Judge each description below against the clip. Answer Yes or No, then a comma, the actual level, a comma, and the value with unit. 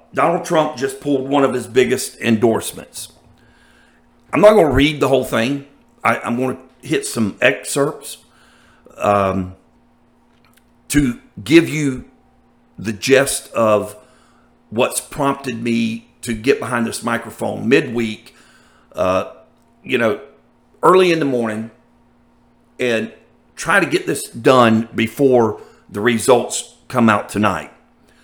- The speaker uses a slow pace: Yes, slow, 125 wpm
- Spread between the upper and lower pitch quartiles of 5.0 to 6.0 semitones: No, average, 3.7 semitones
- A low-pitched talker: Yes, low, 125 Hz